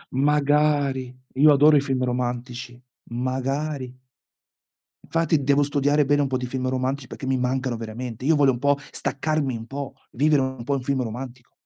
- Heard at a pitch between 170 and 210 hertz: No, low, 135 Hz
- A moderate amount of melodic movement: No, narrow, 2.3 semitones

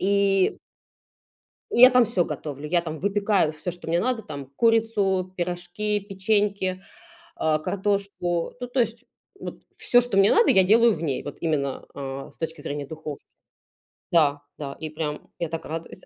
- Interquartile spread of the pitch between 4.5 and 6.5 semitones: Yes, average, 4.9 semitones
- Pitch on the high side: No, medium, 180 Hz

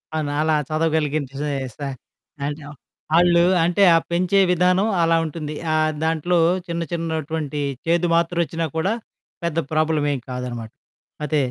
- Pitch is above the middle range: No, medium, 160 Hz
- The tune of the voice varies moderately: No, narrow, 2.3 semitones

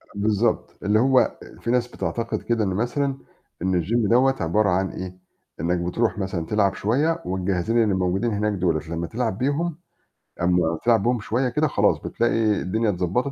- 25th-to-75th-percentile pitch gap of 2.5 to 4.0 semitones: No, average, 4.7 semitones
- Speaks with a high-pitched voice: No, low, 105 Hz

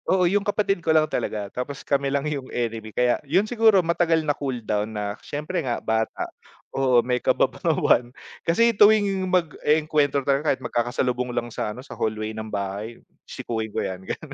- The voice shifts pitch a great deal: Yes, wide, 6.3 semitones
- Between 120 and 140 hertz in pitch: Yes, low, 135 Hz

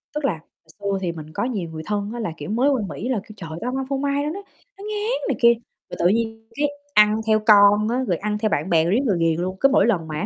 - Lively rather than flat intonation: Yes, wide, 6.0 semitones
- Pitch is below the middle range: No, high, 215 Hz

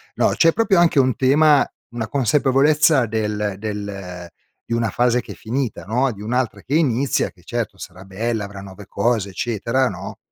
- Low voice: Yes, low, 115 Hz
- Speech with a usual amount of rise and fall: Yes, average, 4.7 semitones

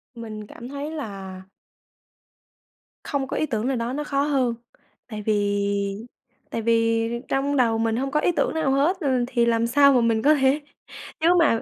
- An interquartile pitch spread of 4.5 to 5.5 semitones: No, average, 3.9 semitones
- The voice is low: No, high, 240 Hz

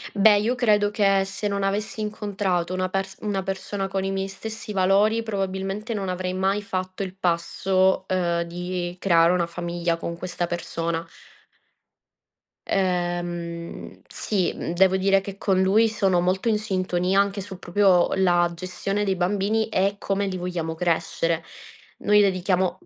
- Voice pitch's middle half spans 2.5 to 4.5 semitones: No, narrow, 2.1 semitones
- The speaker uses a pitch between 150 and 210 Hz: Yes, high, 190 Hz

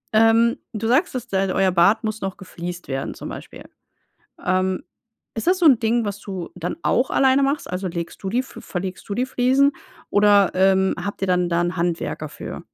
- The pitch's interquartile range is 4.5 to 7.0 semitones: Yes, average, 4.8 semitones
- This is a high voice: Yes, high, 200 Hz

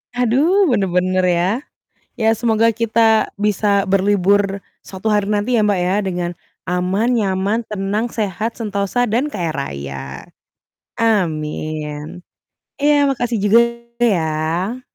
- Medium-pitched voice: No, high, 200 Hz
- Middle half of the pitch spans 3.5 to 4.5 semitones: Yes, average, 4.0 semitones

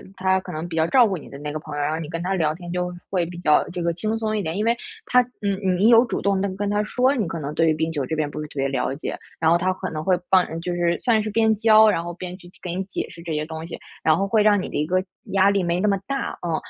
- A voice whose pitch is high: No, medium, 180 Hz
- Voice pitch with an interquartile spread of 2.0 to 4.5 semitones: Yes, average, 3.9 semitones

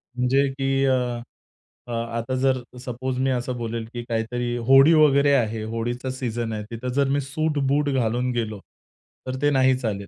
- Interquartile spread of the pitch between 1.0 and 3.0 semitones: Yes, narrow, 2.5 semitones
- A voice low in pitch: Yes, low, 125 Hz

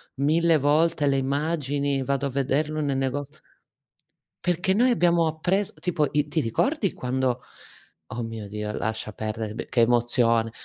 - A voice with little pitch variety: No, average, 5.0 semitones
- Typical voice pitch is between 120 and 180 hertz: Yes, medium, 140 Hz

